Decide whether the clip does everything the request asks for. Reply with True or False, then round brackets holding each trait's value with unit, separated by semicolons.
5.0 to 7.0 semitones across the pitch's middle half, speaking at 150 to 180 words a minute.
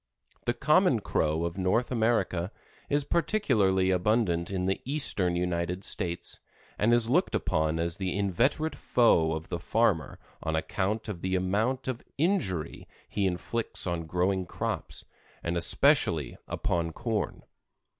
False (5.5 semitones; 135 wpm)